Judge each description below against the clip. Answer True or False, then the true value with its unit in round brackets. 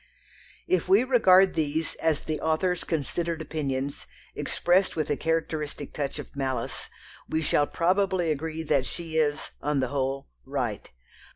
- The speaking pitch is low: False (155 Hz)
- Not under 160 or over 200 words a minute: False (145 wpm)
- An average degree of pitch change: True (3.1 semitones)